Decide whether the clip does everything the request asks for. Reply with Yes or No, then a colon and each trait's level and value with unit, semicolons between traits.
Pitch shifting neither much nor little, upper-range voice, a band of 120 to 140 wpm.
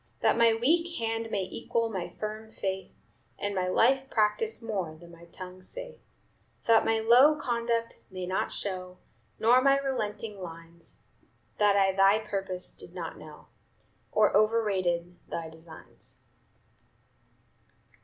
Yes: average, 3.9 semitones; high, 210 Hz; slow, 135 wpm